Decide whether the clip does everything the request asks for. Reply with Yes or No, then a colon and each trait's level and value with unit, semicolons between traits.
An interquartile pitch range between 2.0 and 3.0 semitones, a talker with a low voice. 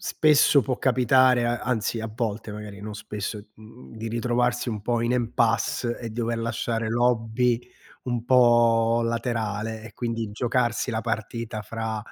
No: narrow, 1.6 semitones; low, 115 Hz